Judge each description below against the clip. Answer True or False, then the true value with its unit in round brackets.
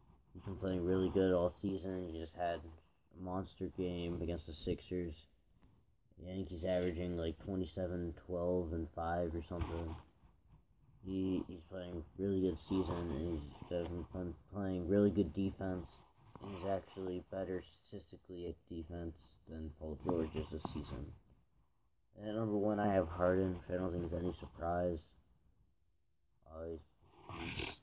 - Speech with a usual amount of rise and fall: False (2.1 semitones)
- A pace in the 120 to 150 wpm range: True (140 wpm)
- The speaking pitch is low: True (90 Hz)